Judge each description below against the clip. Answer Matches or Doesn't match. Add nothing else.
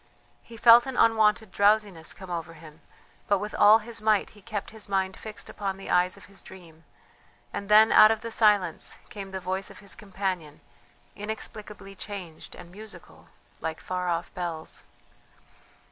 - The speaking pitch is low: Doesn't match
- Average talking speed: Matches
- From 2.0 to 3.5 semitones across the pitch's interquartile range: Matches